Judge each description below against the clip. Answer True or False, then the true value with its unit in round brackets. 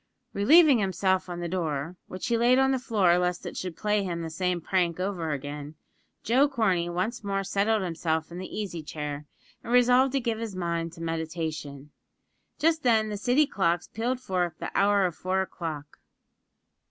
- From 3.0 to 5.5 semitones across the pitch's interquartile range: True (5.0 semitones)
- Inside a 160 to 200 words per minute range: True (180 wpm)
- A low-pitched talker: False (185 Hz)